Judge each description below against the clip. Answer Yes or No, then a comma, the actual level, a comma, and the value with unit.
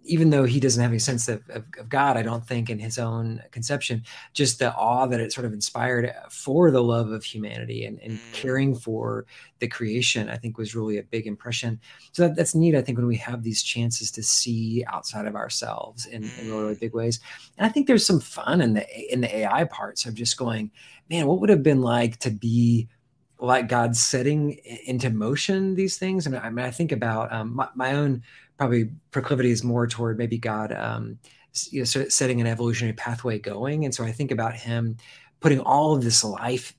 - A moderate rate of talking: No, fast, 220 wpm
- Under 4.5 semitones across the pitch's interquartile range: Yes, average, 2.9 semitones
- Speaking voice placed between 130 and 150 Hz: No, low, 120 Hz